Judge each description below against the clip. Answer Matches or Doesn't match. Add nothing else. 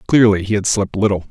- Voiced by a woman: Doesn't match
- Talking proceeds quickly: Matches